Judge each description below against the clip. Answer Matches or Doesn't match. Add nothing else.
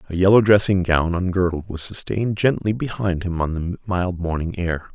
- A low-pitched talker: Matches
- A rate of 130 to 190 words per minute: Matches